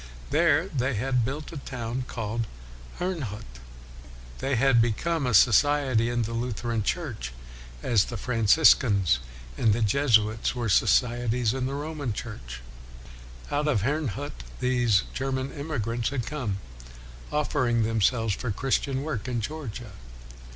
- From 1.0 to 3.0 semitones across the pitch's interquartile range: No, average, 3.9 semitones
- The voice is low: Yes, low, 125 Hz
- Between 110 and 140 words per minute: Yes, slow, 135 wpm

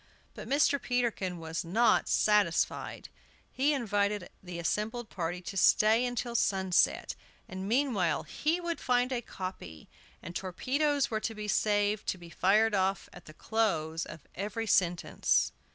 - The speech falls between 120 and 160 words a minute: Yes, average, 145 wpm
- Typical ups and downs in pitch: Yes, average, 4.9 semitones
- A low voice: No, high, 210 Hz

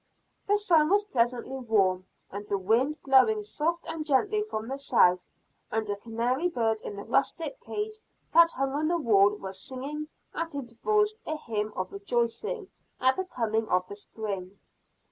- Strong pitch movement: Yes, wide, 7.4 semitones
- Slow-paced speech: No, average, 165 wpm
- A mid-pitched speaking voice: No, very high, 250 Hz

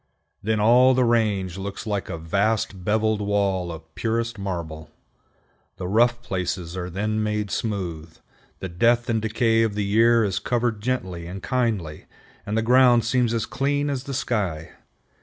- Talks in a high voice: No, low, 105 Hz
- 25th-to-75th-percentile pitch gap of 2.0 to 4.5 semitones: Yes, average, 3.9 semitones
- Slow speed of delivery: No, average, 160 wpm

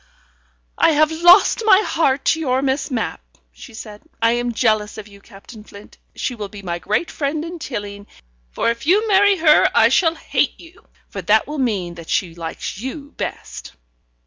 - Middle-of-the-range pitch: No, high, 245 Hz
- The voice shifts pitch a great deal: Yes, wide, 7.4 semitones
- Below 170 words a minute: No, average, 185 wpm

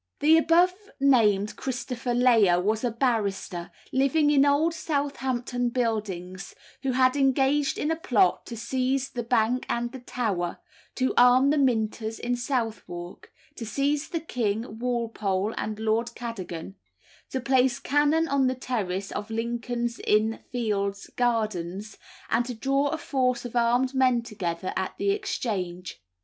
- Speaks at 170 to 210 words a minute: No, average, 145 wpm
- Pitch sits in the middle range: No, high, 240 Hz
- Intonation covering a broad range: No, average, 3.8 semitones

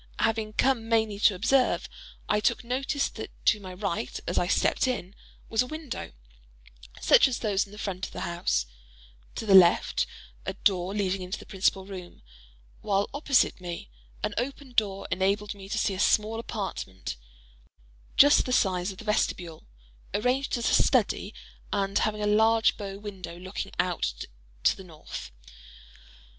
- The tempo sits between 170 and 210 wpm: No, average, 160 wpm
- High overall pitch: Yes, high, 205 Hz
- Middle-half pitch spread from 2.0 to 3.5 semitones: Yes, average, 3.2 semitones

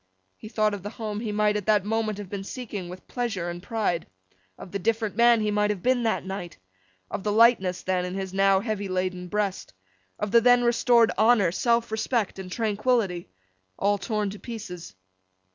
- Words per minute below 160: No, average, 195 wpm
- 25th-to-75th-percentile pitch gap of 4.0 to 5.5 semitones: No, average, 3.0 semitones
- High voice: Yes, high, 210 Hz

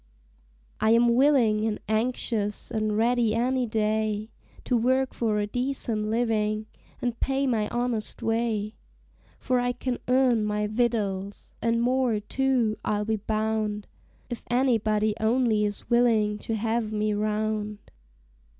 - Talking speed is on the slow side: Yes, slow, 130 wpm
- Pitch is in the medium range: No, high, 220 Hz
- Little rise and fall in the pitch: Yes, narrow, 2.3 semitones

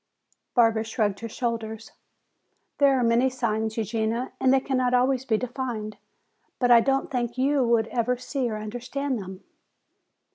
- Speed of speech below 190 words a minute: Yes, average, 150 wpm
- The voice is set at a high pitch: Yes, high, 240 Hz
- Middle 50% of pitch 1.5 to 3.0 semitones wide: Yes, average, 2.7 semitones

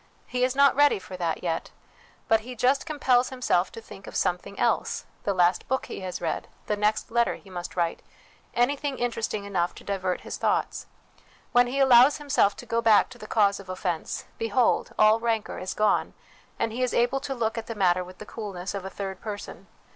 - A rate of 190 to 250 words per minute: Yes, fast, 205 wpm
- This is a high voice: Yes, high, 215 Hz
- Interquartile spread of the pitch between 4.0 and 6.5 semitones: Yes, average, 4.5 semitones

